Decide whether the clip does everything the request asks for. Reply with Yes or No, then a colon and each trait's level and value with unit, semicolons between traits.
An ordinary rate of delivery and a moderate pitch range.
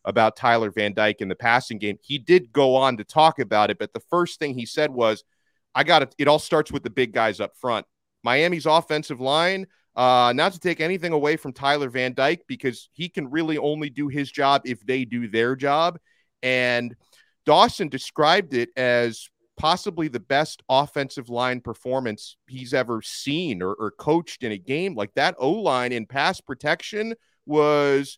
Yes: average, 190 wpm; average, 4.0 semitones